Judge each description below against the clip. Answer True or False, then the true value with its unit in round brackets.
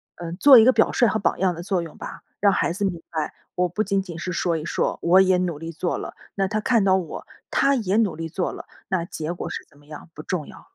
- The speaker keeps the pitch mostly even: False (3.0 semitones)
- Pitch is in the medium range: True (180 Hz)